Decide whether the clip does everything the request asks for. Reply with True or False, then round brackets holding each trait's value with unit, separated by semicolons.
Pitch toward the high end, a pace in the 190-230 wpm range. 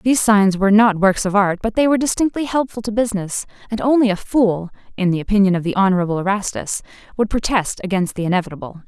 True (205 Hz; 205 wpm)